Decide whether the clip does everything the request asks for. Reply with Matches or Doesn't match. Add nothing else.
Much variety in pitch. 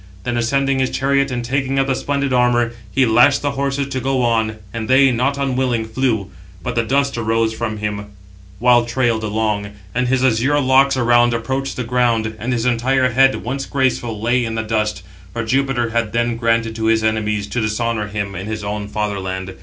Doesn't match